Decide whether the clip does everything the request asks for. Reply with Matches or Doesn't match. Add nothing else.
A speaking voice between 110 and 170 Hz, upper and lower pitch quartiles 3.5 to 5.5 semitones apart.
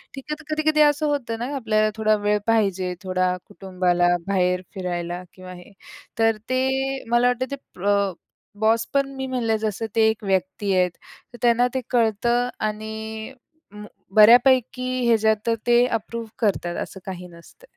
Doesn't match